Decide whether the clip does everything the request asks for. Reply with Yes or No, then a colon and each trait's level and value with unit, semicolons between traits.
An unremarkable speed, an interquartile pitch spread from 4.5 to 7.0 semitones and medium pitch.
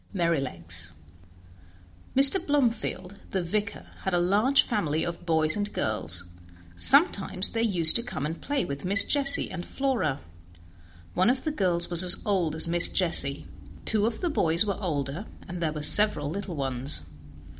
Yes: average, 165 wpm; wide, 5.5 semitones; medium, 180 Hz